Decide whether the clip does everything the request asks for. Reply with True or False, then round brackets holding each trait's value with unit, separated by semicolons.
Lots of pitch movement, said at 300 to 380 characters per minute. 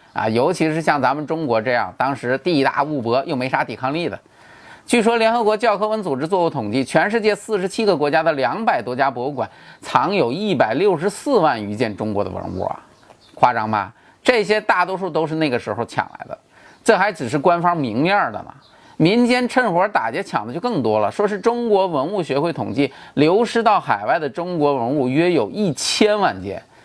True (7.9 semitones; 305 characters per minute)